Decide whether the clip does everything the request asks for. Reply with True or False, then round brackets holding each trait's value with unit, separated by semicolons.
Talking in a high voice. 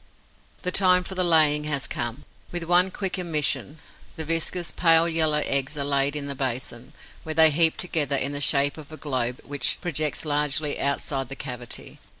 False (150 Hz)